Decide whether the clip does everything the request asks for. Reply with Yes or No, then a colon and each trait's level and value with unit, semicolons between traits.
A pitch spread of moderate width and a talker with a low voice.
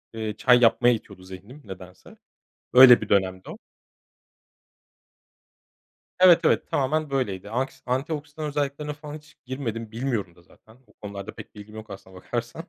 No: wide, 6.0 semitones; low, 120 Hz